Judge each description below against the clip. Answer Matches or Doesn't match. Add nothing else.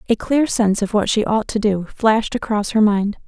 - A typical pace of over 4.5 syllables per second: Matches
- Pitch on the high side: Matches